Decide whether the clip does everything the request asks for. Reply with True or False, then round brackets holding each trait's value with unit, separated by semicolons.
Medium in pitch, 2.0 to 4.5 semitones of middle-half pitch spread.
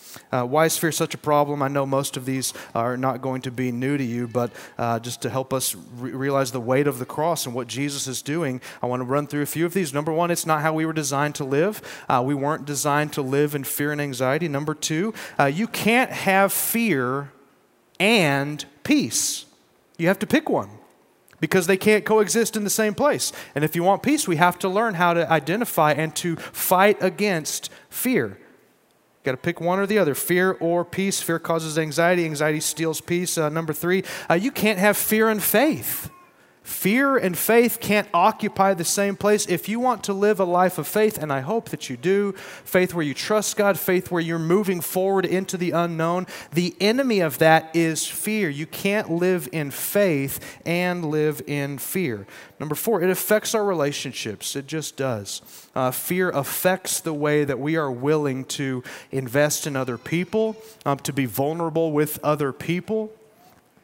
False (165 Hz; 5.5 semitones)